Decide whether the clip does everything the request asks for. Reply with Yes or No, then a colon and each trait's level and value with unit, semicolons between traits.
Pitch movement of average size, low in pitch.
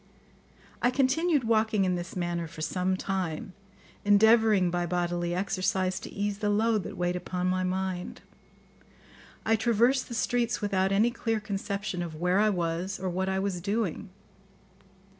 No: average, 3.3 semitones; high, 190 Hz